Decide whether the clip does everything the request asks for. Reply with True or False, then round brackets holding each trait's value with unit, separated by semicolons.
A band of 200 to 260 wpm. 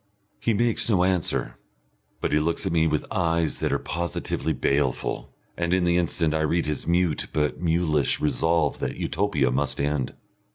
False (170 wpm)